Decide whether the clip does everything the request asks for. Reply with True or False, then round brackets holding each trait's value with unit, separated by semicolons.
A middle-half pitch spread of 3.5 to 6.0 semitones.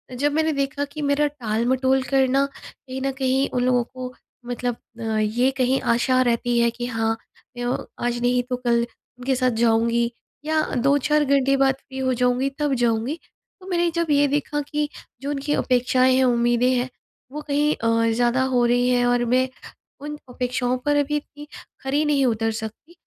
False (2.7 semitones)